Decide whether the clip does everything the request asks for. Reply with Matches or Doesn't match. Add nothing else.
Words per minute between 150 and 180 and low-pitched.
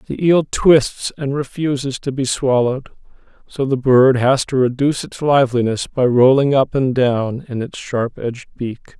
Matches